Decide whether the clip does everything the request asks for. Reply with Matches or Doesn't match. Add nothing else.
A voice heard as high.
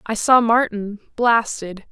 Matches